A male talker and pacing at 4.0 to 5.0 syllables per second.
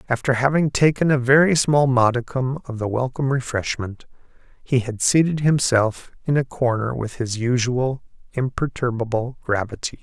Yes: male; 4.9 syllables/s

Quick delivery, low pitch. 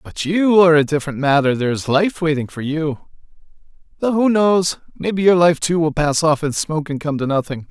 No: fast, 220 wpm; medium, 160 Hz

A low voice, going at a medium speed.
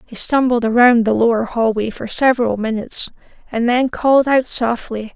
No: high, 235 Hz; average, 165 wpm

